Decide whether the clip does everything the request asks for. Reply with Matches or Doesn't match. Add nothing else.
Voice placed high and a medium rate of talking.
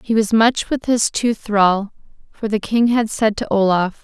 Doesn't match